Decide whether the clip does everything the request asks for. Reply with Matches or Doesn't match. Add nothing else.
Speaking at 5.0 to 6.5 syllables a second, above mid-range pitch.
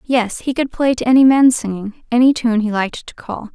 Matches